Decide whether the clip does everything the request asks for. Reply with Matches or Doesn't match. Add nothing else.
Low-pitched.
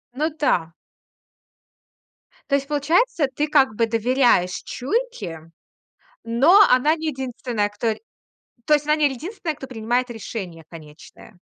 Doesn't match